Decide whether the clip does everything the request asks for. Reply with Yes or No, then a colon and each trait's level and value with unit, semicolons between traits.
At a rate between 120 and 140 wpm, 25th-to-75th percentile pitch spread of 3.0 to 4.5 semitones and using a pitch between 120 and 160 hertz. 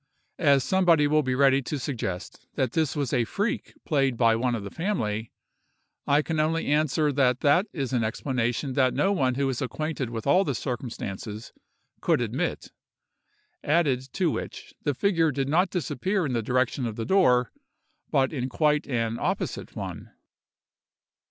No: average, 165 wpm; average, 3.9 semitones; low, 135 Hz